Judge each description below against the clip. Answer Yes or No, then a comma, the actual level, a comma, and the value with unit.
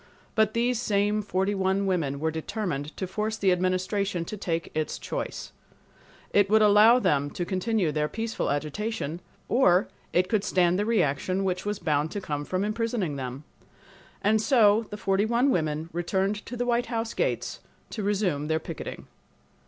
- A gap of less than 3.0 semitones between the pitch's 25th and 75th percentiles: No, average, 4.6 semitones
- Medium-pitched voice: No, high, 195 Hz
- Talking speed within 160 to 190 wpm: Yes, average, 170 wpm